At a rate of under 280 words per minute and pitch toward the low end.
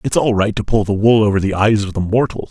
No: fast, 310 wpm; low, 105 Hz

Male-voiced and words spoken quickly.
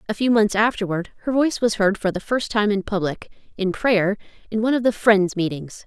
No: female; fast, 225 wpm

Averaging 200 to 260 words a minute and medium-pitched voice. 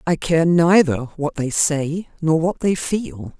No: average, 175 wpm; medium, 155 Hz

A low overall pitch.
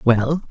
Yes: low, 130 Hz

